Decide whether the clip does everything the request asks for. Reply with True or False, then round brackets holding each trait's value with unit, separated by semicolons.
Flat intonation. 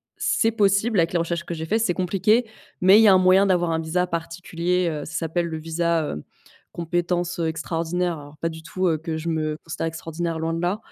True (2.0 semitones)